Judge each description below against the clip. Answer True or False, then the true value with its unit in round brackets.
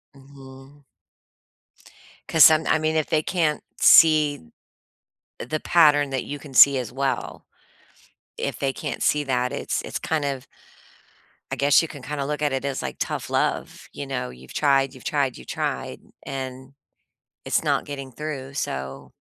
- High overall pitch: False (140 Hz)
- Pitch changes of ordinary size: False (2.2 semitones)